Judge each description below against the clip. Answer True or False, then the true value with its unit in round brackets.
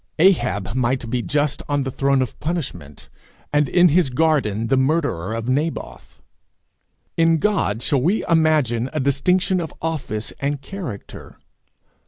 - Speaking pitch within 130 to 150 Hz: True (140 Hz)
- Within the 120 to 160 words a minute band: True (140 wpm)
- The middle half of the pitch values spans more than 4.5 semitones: True (5.1 semitones)